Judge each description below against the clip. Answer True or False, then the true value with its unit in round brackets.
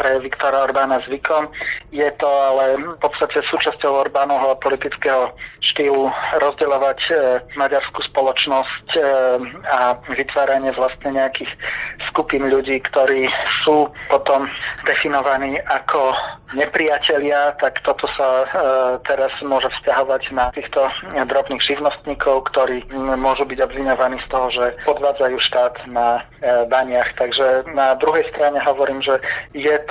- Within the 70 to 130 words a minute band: True (125 wpm)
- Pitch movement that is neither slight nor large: False (1.4 semitones)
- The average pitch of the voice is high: False (135 Hz)